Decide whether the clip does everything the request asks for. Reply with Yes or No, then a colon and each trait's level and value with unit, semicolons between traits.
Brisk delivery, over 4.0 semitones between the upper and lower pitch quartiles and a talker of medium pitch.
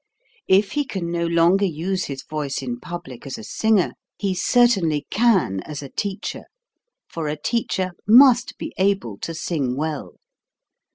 No: average, 155 wpm; average, 5.2 semitones; medium, 175 Hz